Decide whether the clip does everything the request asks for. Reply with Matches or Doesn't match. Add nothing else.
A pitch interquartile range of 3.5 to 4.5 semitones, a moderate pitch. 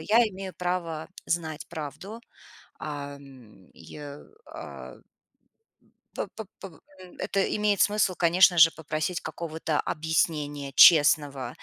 Matches